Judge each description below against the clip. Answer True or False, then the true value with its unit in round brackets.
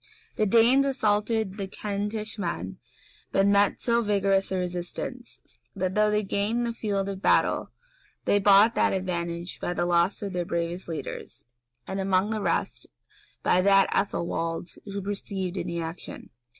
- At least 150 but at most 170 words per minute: True (165 wpm)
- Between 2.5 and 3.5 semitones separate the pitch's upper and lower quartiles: True (2.8 semitones)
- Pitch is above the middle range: True (195 Hz)